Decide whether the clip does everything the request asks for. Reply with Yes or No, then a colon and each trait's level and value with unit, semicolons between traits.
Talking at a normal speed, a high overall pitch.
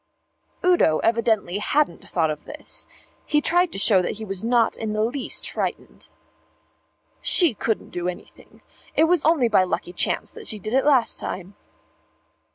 Yes: average, 165 wpm; high, 220 Hz